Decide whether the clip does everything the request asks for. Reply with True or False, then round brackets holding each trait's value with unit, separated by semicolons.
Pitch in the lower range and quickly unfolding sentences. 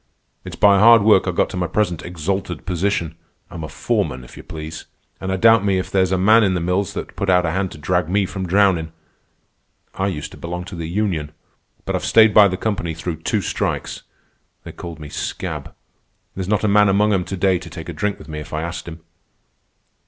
True (90 Hz; 225 wpm)